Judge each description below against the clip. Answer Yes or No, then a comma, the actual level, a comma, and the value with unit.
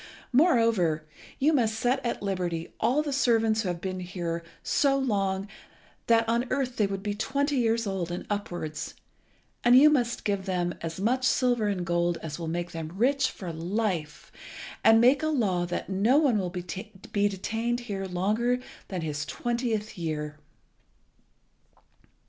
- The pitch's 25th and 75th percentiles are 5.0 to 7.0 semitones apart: Yes, wide, 5.4 semitones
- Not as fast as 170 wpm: Yes, average, 160 wpm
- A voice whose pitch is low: No, high, 205 Hz